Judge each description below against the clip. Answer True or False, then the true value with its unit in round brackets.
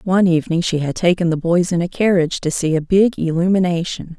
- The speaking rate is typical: False (215 wpm)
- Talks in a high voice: False (175 Hz)